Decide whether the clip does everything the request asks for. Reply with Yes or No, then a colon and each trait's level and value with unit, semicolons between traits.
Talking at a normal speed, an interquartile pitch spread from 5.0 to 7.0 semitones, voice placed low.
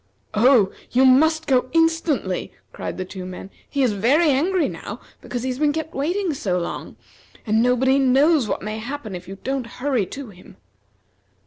No: average, 180 wpm; wide, 5.5 semitones; very high, 260 Hz